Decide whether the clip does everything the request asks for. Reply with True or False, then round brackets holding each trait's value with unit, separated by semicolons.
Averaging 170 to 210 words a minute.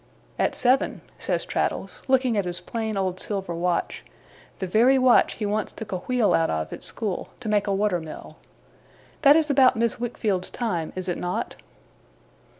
True (175 wpm)